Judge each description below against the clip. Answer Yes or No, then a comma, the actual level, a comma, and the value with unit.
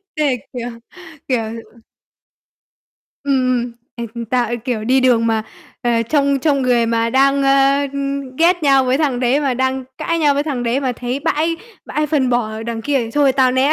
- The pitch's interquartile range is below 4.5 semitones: Yes, narrow, 2.6 semitones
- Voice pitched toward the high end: Yes, very high, 260 Hz